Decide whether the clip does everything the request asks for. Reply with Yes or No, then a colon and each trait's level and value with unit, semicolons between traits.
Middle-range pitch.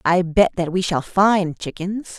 Yes: medium, 180 Hz